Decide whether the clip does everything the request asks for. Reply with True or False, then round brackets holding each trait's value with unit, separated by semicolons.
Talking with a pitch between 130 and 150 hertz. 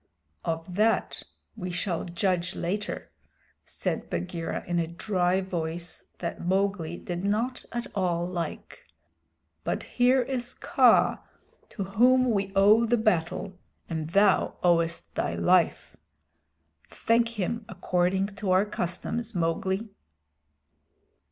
False (185 Hz)